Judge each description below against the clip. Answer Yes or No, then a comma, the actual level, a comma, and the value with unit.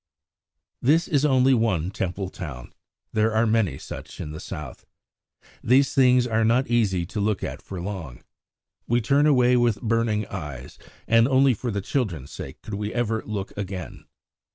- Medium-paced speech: Yes, average, 165 wpm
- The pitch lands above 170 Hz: No, low, 110 Hz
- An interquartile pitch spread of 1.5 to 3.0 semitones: No, average, 4.6 semitones